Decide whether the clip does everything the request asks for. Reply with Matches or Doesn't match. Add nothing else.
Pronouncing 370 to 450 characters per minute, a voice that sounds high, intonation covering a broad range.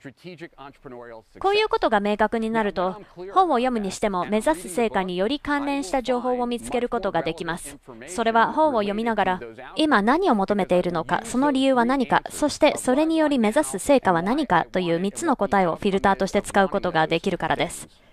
Matches